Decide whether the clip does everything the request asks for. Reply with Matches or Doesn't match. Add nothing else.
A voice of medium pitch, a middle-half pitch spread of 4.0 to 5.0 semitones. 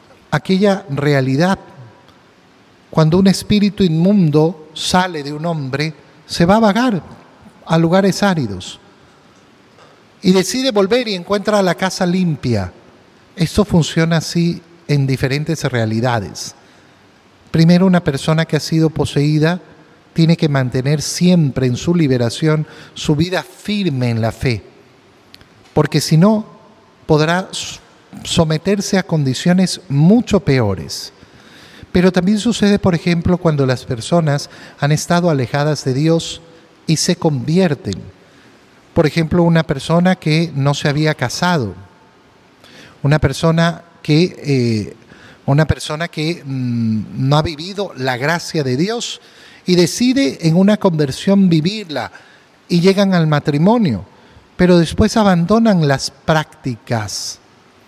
Matches